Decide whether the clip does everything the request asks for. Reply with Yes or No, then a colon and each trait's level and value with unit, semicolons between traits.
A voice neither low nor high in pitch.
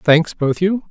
Yes: medium, 170 Hz